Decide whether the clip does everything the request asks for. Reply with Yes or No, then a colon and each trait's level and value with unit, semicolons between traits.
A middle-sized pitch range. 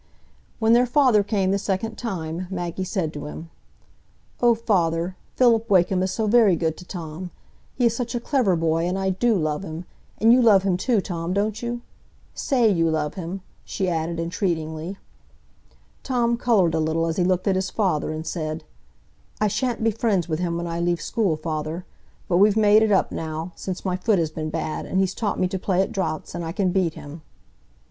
Yes: average, 4.4 semitones